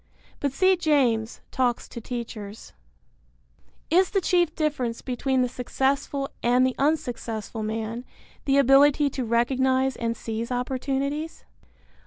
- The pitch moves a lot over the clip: No, average, 3.2 semitones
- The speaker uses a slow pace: Yes, slow, 120 wpm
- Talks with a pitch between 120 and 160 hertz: No, very high, 260 Hz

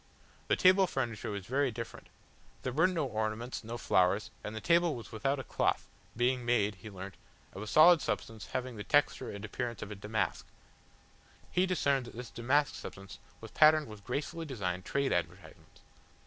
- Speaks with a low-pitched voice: Yes, low, 120 Hz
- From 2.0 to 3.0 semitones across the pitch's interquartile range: No, average, 5.1 semitones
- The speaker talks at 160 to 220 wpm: Yes, average, 175 wpm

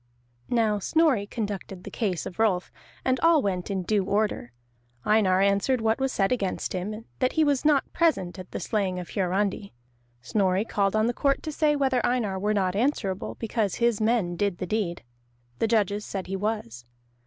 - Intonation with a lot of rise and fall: No, average, 3.9 semitones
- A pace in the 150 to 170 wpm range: No, average, 185 wpm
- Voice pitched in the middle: No, high, 210 Hz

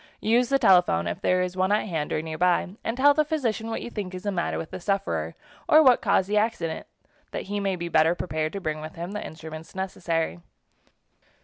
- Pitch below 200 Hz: Yes, medium, 185 Hz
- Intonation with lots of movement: No, average, 4.6 semitones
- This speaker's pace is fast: Yes, fast, 220 wpm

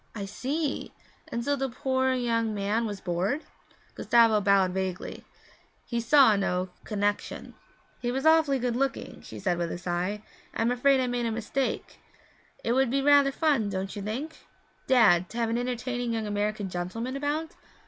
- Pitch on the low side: No, high, 230 Hz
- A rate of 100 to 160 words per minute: No, average, 170 wpm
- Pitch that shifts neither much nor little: Yes, average, 4.6 semitones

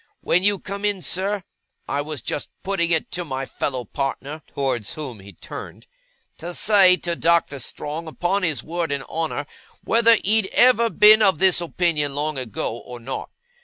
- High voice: No, medium, 165 Hz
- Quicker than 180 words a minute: No, average, 170 wpm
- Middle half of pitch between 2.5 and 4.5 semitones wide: No, average, 5.3 semitones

